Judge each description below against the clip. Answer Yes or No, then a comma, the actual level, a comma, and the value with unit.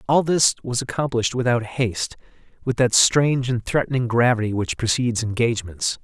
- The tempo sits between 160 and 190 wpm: No, average, 150 wpm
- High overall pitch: No, low, 120 Hz